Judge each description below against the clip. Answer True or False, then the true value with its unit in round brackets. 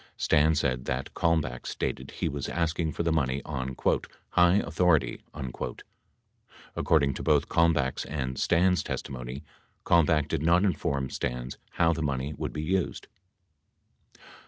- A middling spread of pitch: True (4.0 semitones)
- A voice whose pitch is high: False (75 Hz)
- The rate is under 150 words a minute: True (135 wpm)